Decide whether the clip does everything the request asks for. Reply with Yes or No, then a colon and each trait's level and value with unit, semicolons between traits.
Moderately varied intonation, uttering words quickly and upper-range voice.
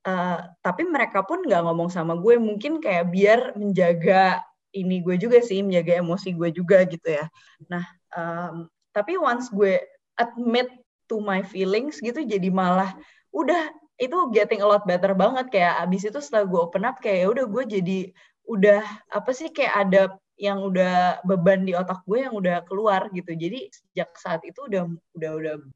Yes: average, 4.1 semitones; fast, 170 wpm; high, 195 Hz